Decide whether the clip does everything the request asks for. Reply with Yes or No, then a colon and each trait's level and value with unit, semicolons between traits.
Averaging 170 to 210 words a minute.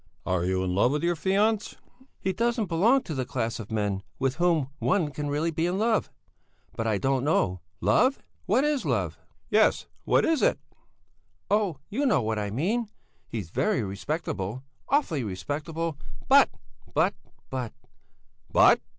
No: average, 160 wpm